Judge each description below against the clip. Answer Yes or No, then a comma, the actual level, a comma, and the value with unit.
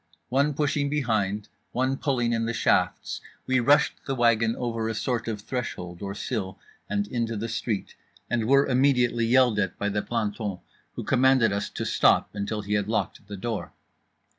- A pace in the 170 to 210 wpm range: Yes, average, 175 wpm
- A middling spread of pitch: Yes, average, 3.6 semitones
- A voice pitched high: No, low, 115 Hz